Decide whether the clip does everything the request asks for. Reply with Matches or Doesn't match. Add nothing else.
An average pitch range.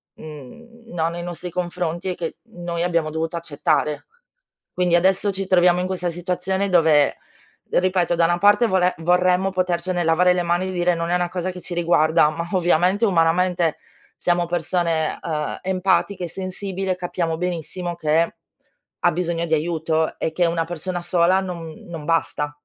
Doesn't match